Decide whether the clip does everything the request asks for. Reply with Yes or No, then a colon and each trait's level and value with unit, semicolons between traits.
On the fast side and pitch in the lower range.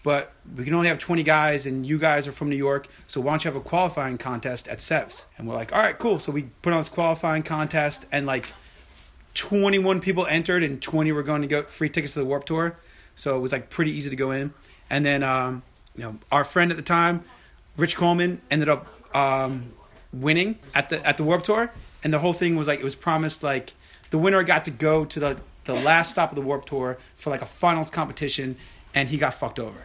No: fast, 240 wpm; medium, 150 Hz